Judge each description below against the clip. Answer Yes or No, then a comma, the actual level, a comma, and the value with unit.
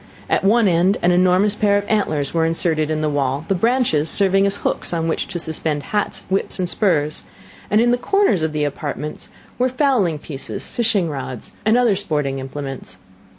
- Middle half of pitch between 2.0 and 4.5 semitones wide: No, average, 5.3 semitones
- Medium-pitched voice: Yes, medium, 175 Hz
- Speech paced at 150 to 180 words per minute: No, average, 190 wpm